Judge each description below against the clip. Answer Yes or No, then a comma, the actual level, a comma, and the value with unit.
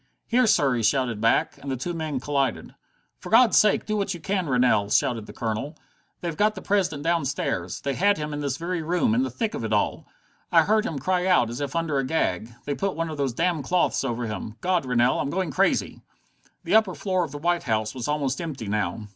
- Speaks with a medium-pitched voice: Yes, medium, 150 Hz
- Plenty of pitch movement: Yes, wide, 6.4 semitones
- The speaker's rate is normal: No, fast, 230 wpm